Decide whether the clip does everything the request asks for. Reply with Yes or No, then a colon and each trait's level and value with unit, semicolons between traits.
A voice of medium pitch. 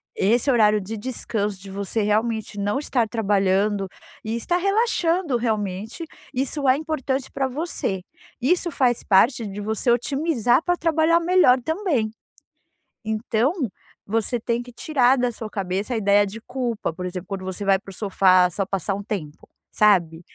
No: high, 225 Hz